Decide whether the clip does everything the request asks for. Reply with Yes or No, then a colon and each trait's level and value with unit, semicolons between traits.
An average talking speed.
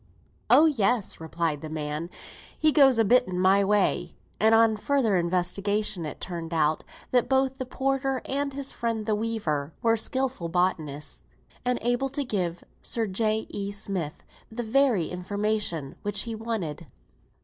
Yes: average, 155 wpm